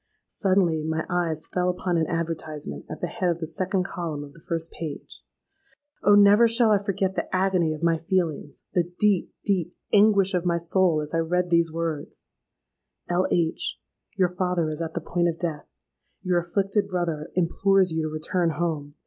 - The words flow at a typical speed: Yes, average, 175 wpm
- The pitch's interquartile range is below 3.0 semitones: Yes, narrow, 2.5 semitones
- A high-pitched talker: No, medium, 175 Hz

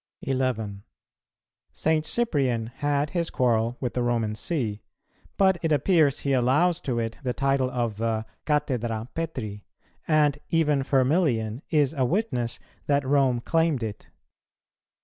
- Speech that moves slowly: Yes, slow, 130 wpm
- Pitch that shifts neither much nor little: Yes, average, 4.3 semitones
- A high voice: No, low, 130 Hz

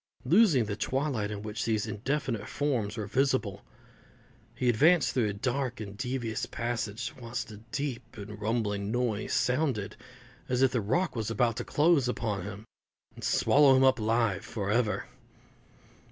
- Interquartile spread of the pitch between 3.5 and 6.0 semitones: Yes, average, 3.8 semitones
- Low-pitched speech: Yes, low, 115 Hz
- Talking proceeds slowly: No, average, 155 wpm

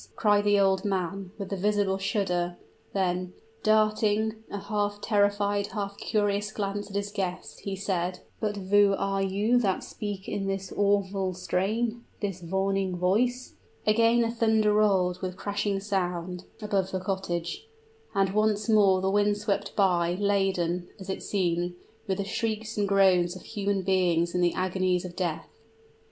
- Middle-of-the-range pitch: No, high, 195 Hz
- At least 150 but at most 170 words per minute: Yes, average, 155 wpm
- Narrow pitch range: Yes, narrow, 1.9 semitones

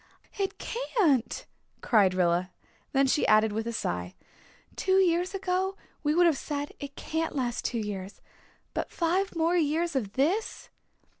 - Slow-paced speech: No, average, 150 wpm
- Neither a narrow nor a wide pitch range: No, wide, 8.3 semitones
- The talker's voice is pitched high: Yes, very high, 290 Hz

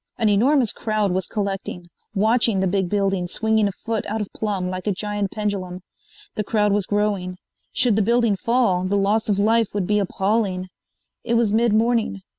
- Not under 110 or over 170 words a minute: No, average, 185 wpm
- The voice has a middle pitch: No, high, 205 Hz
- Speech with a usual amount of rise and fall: No, narrow, 2.3 semitones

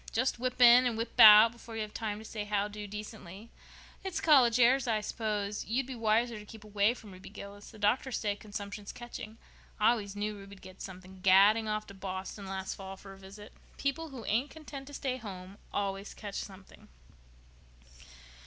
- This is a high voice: Yes, high, 210 Hz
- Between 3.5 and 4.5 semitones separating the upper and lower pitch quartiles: No, average, 2.8 semitones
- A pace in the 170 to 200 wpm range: Yes, average, 190 wpm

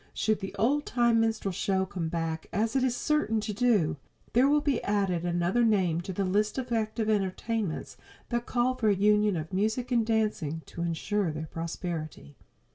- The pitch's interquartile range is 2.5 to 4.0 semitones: No, average, 4.8 semitones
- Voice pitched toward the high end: Yes, high, 210 Hz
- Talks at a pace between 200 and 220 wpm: No, average, 185 wpm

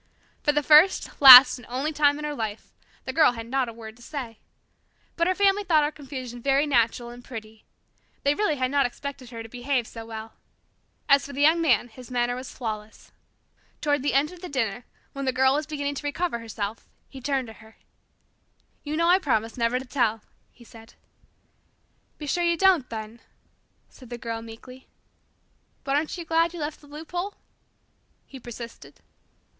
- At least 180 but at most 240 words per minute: Yes, average, 190 wpm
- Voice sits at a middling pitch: No, very high, 265 Hz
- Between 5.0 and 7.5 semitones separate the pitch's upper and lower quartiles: No, average, 4.3 semitones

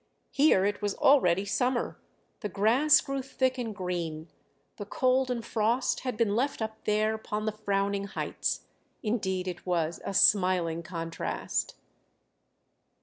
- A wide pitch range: No, average, 4.6 semitones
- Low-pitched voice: No, high, 210 Hz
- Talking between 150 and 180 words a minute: No, average, 140 wpm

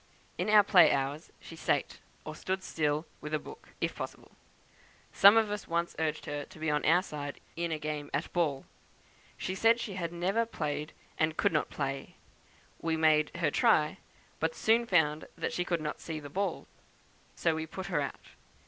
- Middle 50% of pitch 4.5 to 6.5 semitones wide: No, average, 3.8 semitones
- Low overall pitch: No, medium, 160 Hz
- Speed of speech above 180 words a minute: Yes, average, 190 wpm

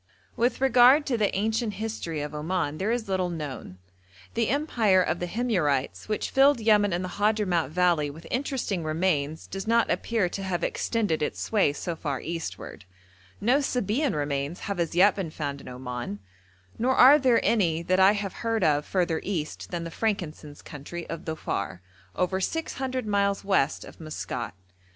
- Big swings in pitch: Yes, wide, 6.0 semitones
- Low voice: No, medium, 185 Hz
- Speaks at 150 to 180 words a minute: Yes, average, 175 wpm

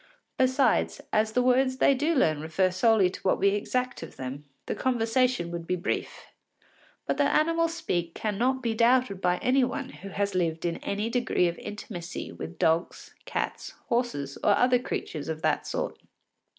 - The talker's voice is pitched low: No, high, 215 Hz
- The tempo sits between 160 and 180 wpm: Yes, average, 175 wpm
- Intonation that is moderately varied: No, wide, 6.6 semitones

